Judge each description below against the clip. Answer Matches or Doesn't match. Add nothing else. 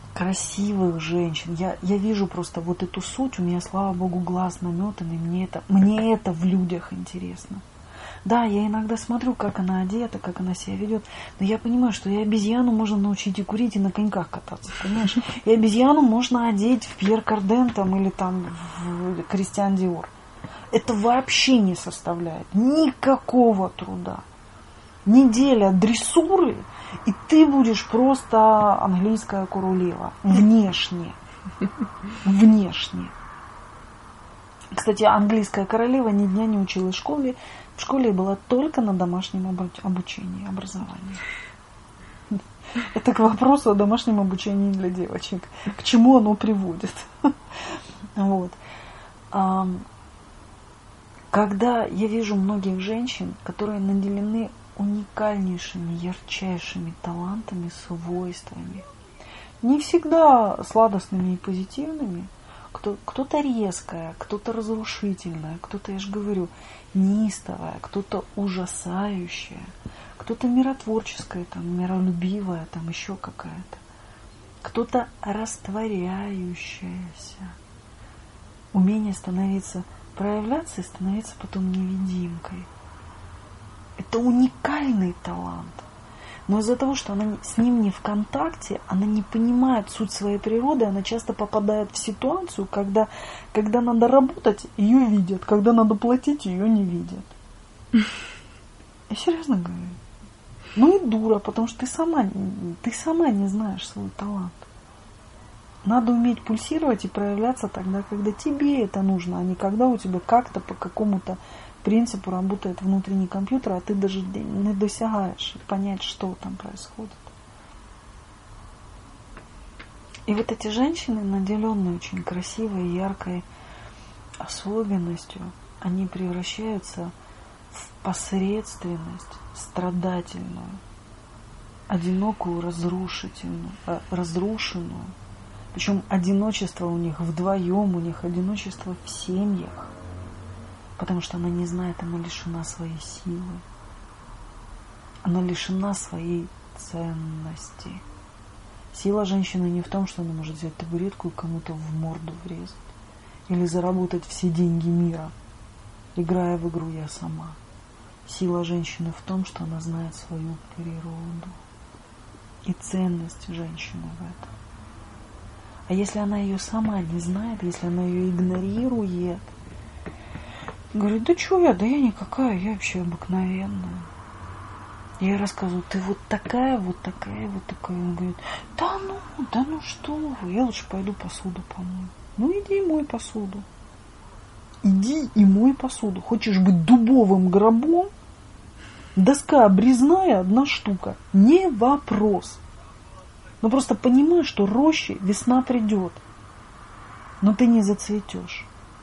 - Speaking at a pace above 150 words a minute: Doesn't match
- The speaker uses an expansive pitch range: Doesn't match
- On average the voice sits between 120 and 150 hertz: Doesn't match